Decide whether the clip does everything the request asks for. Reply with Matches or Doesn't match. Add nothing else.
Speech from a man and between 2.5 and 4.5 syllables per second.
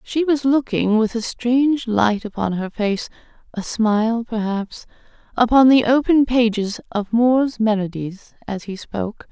Doesn't match